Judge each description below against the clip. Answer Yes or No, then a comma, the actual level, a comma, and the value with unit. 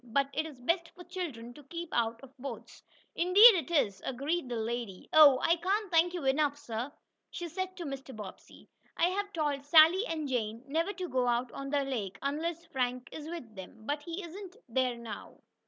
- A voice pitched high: Yes, very high, 290 Hz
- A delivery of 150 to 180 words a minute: No, average, 200 wpm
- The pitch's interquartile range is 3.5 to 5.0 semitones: No, wide, 5.6 semitones